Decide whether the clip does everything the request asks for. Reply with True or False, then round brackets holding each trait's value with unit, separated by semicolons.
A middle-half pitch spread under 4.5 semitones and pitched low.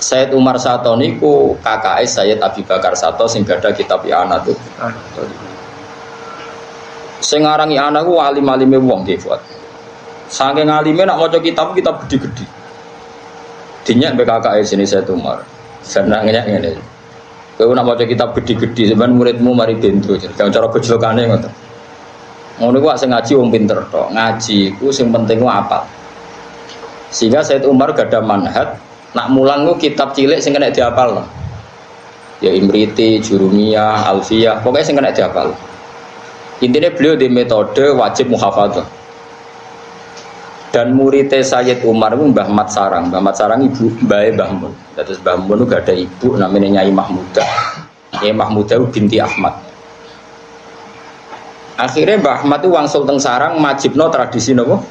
True (4.0 semitones; 120 Hz)